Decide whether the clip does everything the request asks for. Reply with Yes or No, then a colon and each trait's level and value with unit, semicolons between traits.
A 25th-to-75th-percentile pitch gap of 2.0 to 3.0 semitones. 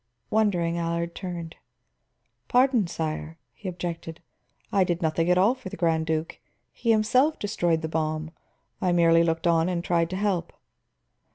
Yes: narrow, 2.5 semitones